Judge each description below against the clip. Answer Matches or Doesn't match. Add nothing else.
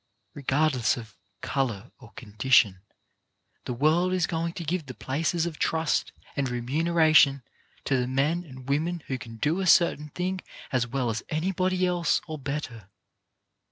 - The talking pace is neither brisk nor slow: Matches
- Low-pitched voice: Doesn't match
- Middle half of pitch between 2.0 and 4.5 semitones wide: Doesn't match